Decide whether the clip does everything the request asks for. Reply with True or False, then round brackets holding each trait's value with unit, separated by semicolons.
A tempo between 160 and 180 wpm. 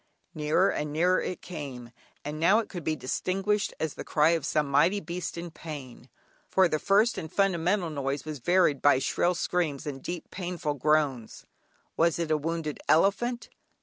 True (175 wpm)